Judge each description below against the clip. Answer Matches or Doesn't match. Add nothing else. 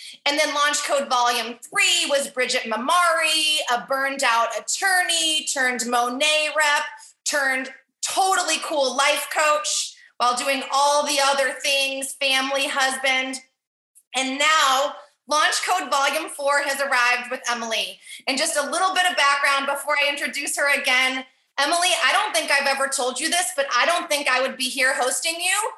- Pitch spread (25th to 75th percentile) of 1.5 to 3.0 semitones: Matches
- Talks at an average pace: Matches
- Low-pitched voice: Doesn't match